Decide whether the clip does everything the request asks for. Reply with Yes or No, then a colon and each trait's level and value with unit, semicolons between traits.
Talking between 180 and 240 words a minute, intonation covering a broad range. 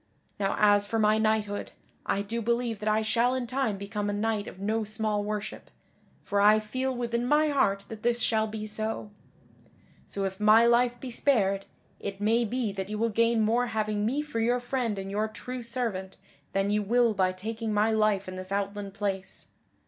No: average, 195 wpm; narrow, 2.5 semitones